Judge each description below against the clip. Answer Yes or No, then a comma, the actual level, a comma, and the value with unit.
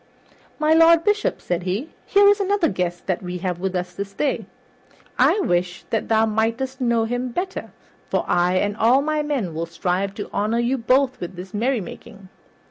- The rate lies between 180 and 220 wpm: Yes, average, 185 wpm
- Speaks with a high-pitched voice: Yes, high, 220 Hz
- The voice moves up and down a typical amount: No, wide, 6.9 semitones